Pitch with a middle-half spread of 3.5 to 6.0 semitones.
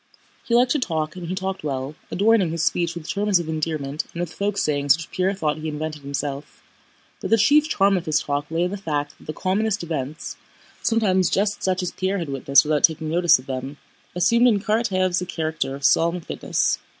Yes: average, 4.2 semitones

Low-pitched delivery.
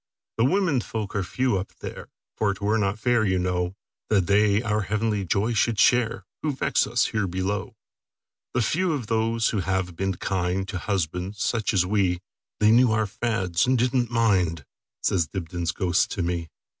Yes: low, 105 Hz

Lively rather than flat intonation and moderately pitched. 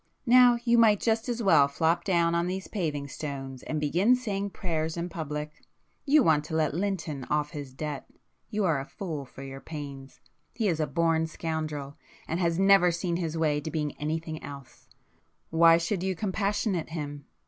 No: average, 4.1 semitones; medium, 165 Hz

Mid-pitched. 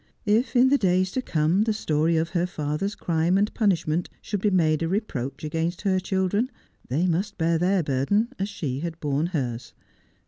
Yes: medium, 175 Hz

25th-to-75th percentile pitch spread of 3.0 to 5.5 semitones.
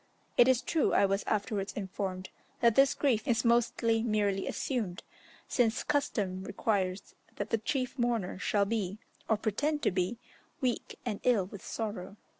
Yes: average, 3.5 semitones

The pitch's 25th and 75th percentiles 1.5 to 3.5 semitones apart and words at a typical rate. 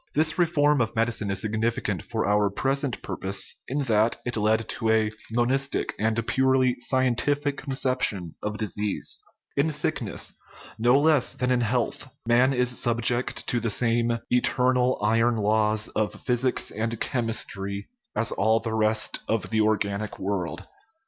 Yes: average, 3.0 semitones; average, 150 wpm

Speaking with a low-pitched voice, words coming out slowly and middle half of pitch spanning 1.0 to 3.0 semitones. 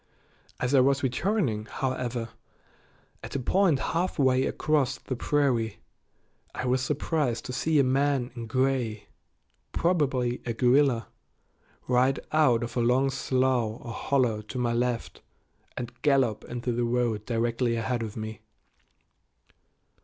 Yes: low, 125 Hz; slow, 130 wpm; narrow, 2.5 semitones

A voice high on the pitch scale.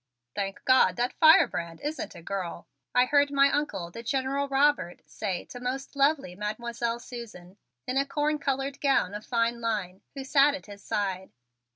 Yes: high, 245 Hz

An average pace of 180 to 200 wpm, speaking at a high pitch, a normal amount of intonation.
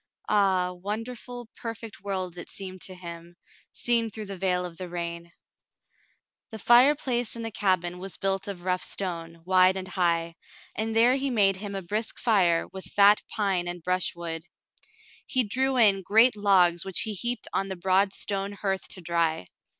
No: average, 170 wpm; high, 195 Hz; average, 3.4 semitones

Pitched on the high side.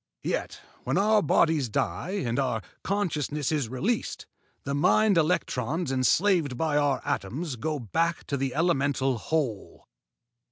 No: medium, 145 Hz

